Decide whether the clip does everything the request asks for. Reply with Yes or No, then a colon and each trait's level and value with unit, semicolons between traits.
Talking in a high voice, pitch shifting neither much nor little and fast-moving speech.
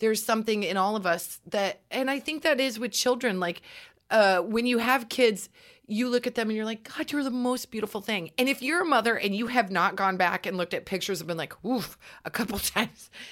Yes: high, 225 Hz; average, 4.5 semitones; fast, 250 wpm